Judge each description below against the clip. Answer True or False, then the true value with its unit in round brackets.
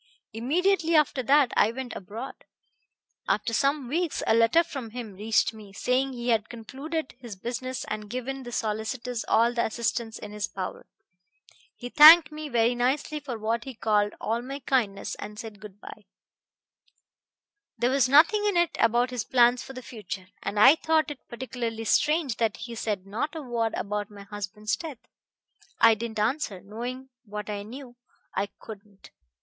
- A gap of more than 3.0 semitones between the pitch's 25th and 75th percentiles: True (4.0 semitones)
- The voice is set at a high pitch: True (235 Hz)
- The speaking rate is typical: True (170 wpm)